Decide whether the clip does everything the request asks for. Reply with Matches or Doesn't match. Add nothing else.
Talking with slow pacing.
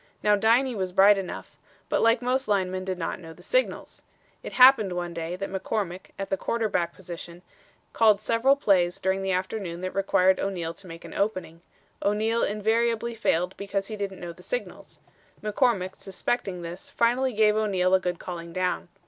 Doesn't match